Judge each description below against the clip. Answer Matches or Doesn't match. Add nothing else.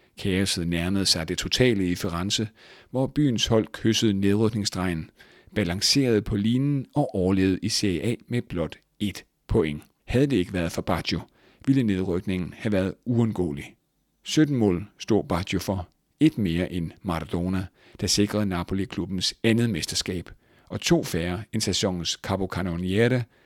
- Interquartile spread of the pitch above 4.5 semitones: Doesn't match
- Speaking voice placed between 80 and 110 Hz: Matches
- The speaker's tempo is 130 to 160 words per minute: Matches